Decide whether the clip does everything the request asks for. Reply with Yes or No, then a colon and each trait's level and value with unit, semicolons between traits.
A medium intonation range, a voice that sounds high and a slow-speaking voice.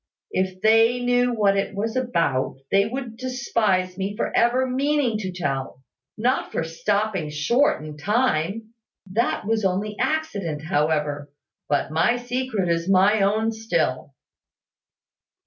No: wide, 6.1 semitones; high, 205 Hz; slow, 130 wpm